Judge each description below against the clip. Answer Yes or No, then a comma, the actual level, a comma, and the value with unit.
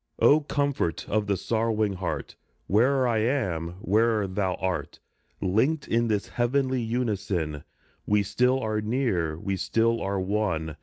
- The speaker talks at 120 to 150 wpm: Yes, average, 140 wpm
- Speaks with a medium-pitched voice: No, low, 105 Hz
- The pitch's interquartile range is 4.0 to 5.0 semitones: Yes, average, 4.3 semitones